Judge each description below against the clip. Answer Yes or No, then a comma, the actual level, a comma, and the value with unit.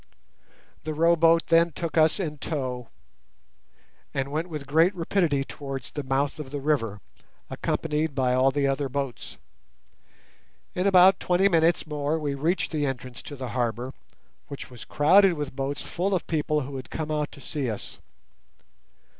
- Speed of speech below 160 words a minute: No, average, 165 wpm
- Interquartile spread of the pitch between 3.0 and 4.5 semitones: Yes, average, 3.5 semitones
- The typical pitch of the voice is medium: Yes, medium, 150 Hz